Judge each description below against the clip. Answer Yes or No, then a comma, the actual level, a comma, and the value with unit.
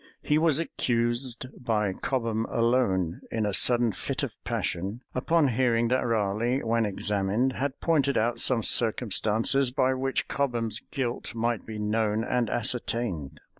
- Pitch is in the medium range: No, low, 115 Hz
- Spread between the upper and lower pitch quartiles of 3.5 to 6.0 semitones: No, average, 3.0 semitones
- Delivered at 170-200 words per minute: No, average, 140 wpm